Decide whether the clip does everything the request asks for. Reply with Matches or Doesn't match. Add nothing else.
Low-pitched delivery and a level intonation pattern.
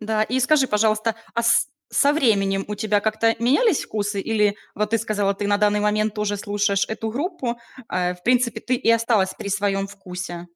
Doesn't match